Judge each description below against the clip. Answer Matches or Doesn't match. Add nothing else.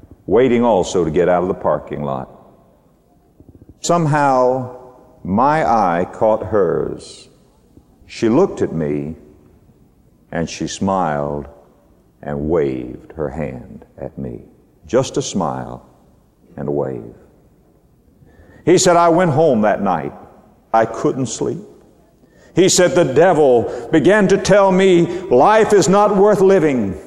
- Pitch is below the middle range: Matches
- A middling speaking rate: Doesn't match